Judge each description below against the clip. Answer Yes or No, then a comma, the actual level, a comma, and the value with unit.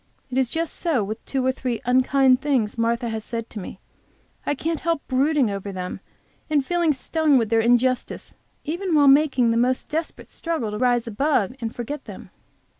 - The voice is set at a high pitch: Yes, very high, 255 Hz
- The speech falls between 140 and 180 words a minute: No, average, 190 wpm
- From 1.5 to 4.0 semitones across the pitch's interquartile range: No, average, 4.4 semitones